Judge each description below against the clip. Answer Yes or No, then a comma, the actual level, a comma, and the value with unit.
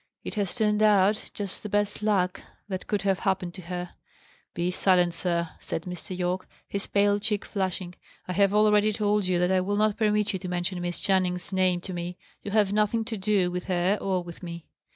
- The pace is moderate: No, fast, 210 wpm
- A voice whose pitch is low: No, high, 190 Hz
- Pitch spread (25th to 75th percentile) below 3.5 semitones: Yes, narrow, 2.5 semitones